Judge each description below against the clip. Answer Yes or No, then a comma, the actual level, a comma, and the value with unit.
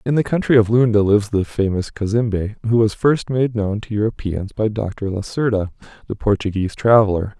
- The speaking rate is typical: Yes, average, 180 wpm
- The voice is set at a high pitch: No, low, 110 Hz